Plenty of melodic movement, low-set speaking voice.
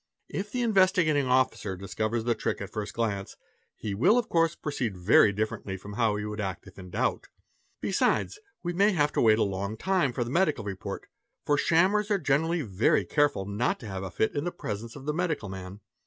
Yes: wide, 8.2 semitones; low, 115 Hz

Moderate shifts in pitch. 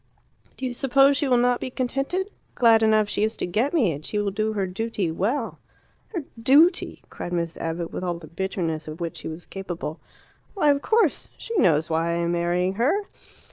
No: wide, 7.5 semitones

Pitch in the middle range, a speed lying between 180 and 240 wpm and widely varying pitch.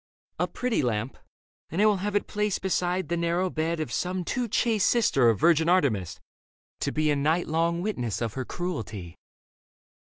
Yes: medium, 170 Hz; average, 185 wpm; wide, 6.1 semitones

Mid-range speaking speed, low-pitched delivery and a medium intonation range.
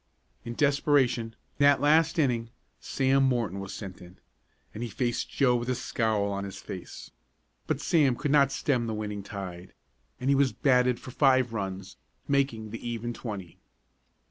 Yes: average, 165 wpm; low, 120 Hz; average, 4.6 semitones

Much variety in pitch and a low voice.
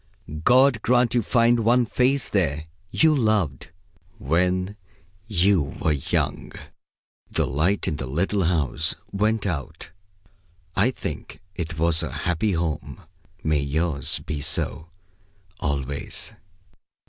Yes: wide, 6.2 semitones; very low, 85 Hz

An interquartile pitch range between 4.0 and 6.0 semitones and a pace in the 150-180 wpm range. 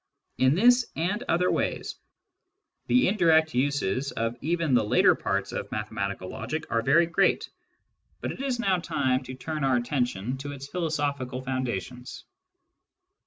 Yes: average, 5.1 semitones; average, 155 wpm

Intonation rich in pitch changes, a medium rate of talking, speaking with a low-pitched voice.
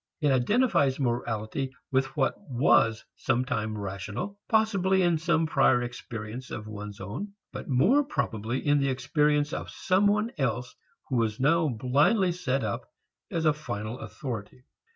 Yes: wide, 6.0 semitones; average, 145 wpm; low, 130 Hz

